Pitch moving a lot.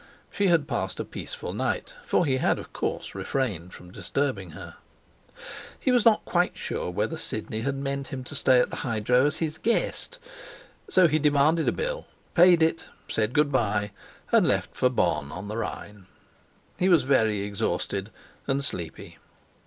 Yes: wide, 7.3 semitones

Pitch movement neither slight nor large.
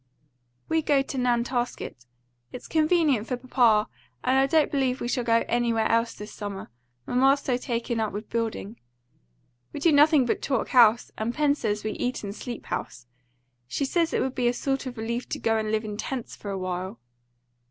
Yes: average, 3.6 semitones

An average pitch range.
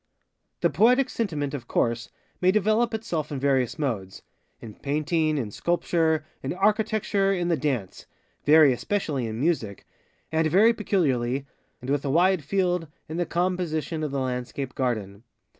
No: wide, 5.8 semitones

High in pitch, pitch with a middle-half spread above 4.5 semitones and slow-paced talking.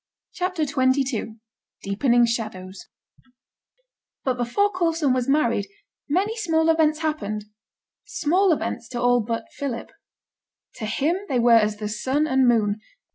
Yes: very high, 255 Hz; wide, 5.5 semitones; slow, 130 wpm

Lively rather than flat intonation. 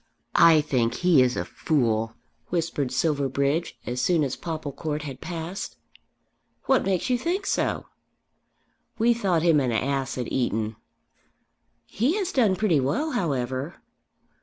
Yes: wide, 5.9 semitones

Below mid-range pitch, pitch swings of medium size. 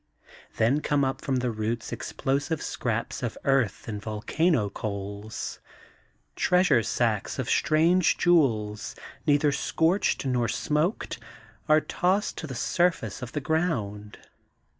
No: low, 130 Hz; wide, 6.3 semitones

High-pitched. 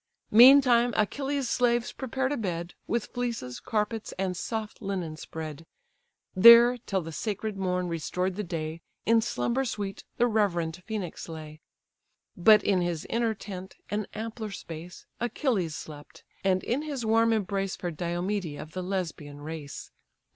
Yes: high, 195 Hz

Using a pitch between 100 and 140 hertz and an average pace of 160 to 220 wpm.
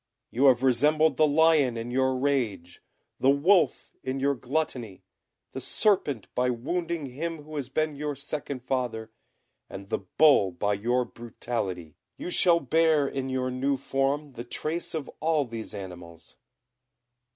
No: low, 135 Hz; average, 150 wpm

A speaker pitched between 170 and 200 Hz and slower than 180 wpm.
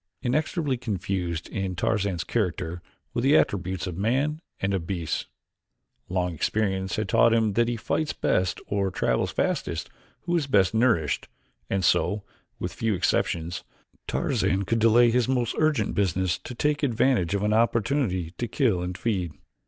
No: low, 105 Hz; average, 155 wpm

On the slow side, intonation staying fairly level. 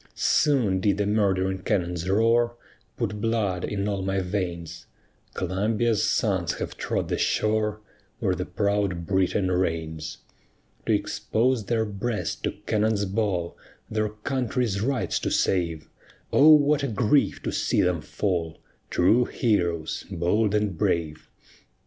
No: slow, 130 wpm; average, 3.6 semitones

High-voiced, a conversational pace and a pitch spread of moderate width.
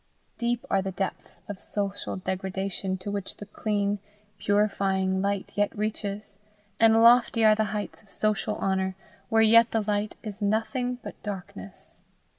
No: high, 205 Hz; average, 150 wpm; narrow, 2.0 semitones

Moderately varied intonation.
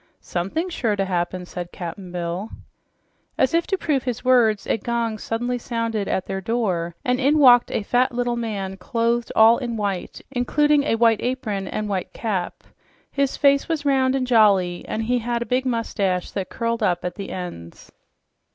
Yes: average, 4.4 semitones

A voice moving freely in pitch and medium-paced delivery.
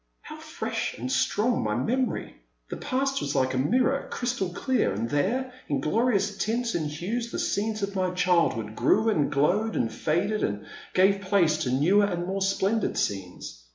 Yes: wide, 7.5 semitones; average, 175 wpm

